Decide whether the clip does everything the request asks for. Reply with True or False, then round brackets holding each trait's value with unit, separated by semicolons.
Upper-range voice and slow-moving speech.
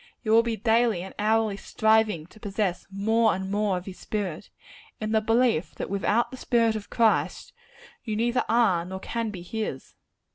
False (215 Hz; 180 wpm)